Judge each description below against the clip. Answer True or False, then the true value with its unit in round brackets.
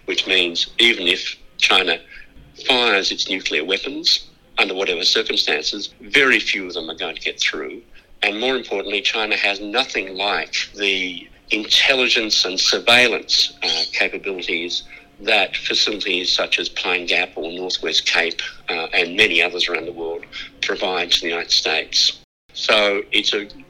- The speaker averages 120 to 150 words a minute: True (145 wpm)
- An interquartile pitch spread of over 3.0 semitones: False (2.5 semitones)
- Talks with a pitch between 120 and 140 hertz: False (95 Hz)